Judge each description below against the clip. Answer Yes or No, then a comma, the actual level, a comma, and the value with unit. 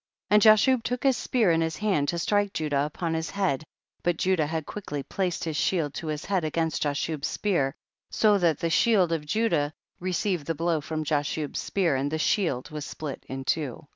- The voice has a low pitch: No, medium, 165 Hz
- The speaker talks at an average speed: No, fast, 215 wpm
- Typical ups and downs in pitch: Yes, average, 4.3 semitones